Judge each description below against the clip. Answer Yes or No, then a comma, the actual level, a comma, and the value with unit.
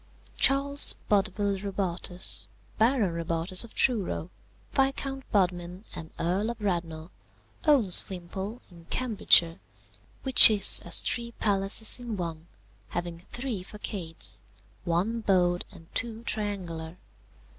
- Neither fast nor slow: No, slow, 110 wpm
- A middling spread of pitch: Yes, average, 4.6 semitones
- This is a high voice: Yes, high, 195 Hz